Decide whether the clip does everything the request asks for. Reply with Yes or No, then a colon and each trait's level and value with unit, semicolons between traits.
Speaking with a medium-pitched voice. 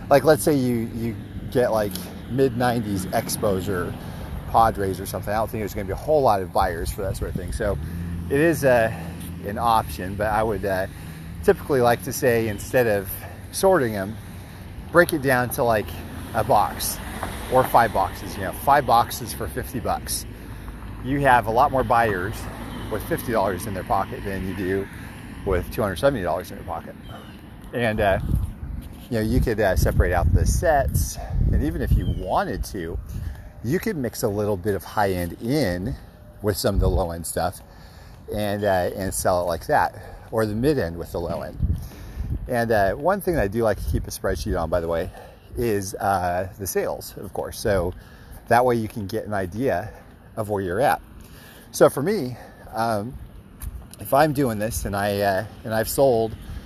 No: low, 100 Hz